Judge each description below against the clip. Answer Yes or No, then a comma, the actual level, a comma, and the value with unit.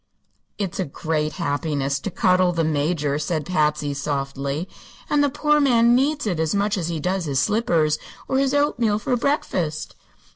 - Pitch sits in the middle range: Yes, medium, 170 Hz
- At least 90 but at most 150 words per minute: No, average, 170 wpm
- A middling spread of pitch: No, wide, 7.1 semitones